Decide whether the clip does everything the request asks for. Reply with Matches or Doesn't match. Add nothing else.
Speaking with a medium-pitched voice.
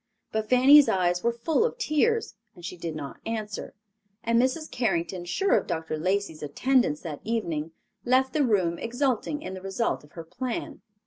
Doesn't match